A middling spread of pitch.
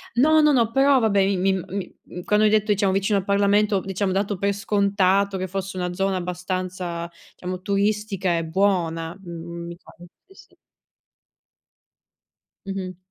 No: narrow, 2.1 semitones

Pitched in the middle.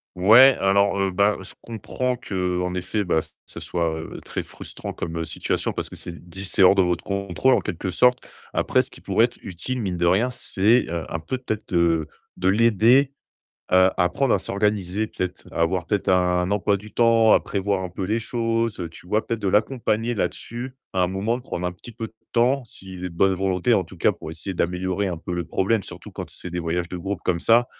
No: very low, 95 Hz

